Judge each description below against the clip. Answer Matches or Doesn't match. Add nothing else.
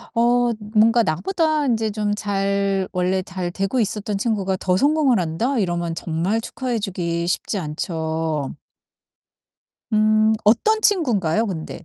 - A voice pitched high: Matches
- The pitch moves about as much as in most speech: Matches